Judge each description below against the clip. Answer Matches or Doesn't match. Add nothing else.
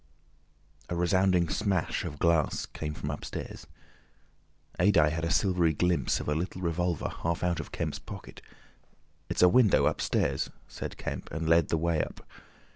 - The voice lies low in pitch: Matches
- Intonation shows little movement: Matches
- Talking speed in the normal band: Matches